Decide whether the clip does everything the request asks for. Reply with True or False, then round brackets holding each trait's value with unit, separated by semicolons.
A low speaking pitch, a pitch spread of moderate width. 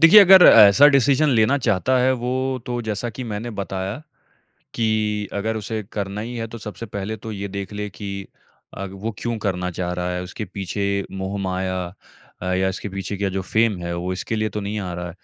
True (105 Hz; 3.1 semitones)